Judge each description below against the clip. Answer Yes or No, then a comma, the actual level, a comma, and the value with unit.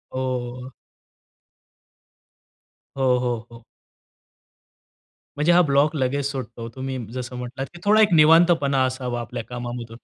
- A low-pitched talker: Yes, low, 130 Hz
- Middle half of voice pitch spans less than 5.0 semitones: Yes, average, 2.9 semitones